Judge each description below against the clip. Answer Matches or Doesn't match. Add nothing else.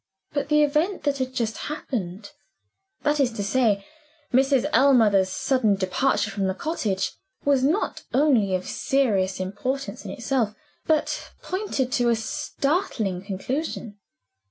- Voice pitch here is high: Matches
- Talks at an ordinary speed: Doesn't match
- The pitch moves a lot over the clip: Matches